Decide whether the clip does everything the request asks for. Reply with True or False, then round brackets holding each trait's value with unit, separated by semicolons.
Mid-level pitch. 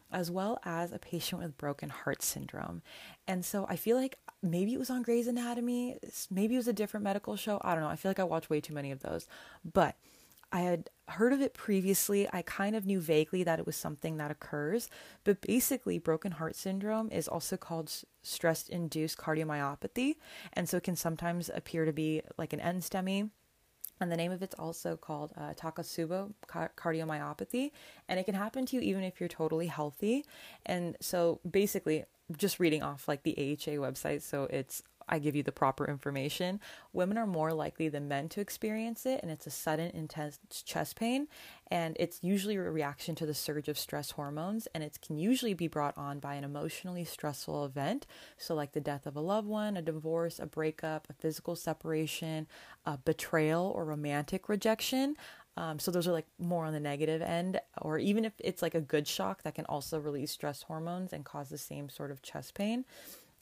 True (170 Hz)